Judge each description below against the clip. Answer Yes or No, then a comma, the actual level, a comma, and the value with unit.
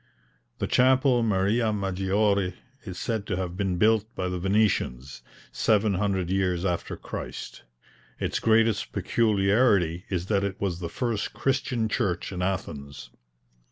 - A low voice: Yes, low, 100 Hz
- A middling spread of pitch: Yes, average, 3.3 semitones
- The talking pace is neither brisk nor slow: No, slow, 130 wpm